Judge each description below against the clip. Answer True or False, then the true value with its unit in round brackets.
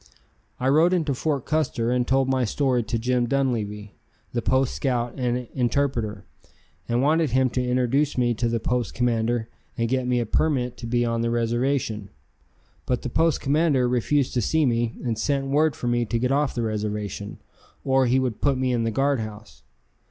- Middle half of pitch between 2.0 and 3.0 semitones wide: True (2.7 semitones)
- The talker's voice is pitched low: True (125 Hz)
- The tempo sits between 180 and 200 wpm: True (190 wpm)